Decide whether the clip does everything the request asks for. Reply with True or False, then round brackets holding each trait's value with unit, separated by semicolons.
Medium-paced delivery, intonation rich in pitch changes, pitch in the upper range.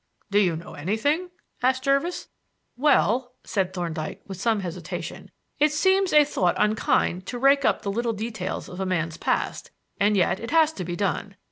True (175 wpm; 7.0 semitones; 215 Hz)